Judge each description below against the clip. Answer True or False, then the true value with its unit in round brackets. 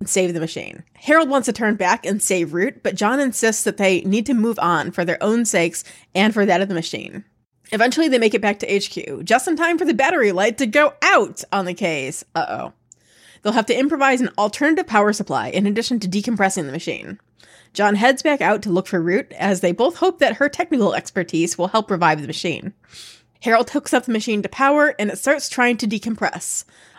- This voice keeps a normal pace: False (225 wpm)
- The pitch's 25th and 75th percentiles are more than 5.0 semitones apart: True (5.6 semitones)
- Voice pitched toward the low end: False (210 Hz)